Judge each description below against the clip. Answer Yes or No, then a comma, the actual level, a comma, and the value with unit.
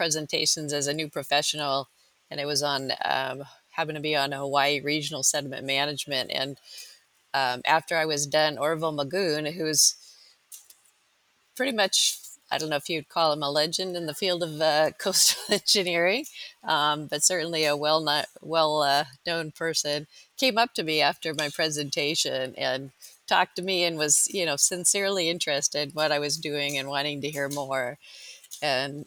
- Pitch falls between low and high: Yes, medium, 150 Hz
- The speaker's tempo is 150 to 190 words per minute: Yes, average, 170 wpm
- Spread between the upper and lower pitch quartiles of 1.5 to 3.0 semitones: Yes, narrow, 2.5 semitones